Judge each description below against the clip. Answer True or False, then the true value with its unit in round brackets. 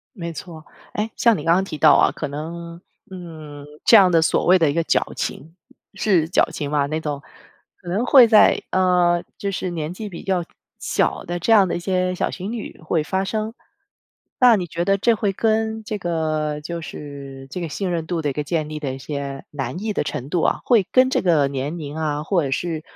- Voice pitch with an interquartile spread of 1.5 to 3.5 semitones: False (4.1 semitones)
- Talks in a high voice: False (170 Hz)